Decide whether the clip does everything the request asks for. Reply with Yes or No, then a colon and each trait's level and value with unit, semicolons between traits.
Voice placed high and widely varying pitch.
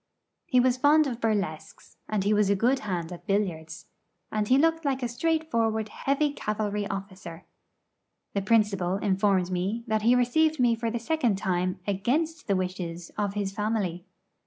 No: high, 210 Hz; average, 4.5 semitones